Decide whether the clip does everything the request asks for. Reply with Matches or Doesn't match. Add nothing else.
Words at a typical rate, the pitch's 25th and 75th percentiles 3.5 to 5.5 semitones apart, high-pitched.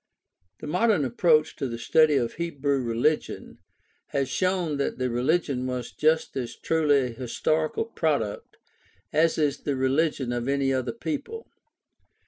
Doesn't match